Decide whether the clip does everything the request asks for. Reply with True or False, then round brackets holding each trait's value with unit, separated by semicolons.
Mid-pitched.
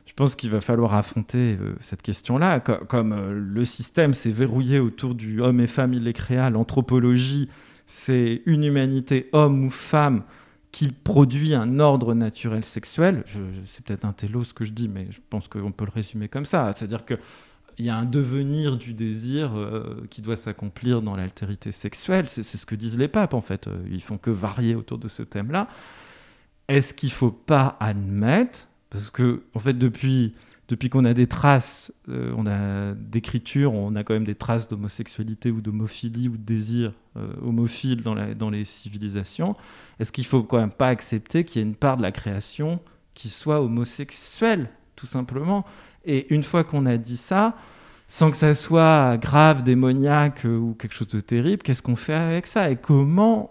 False (120 Hz)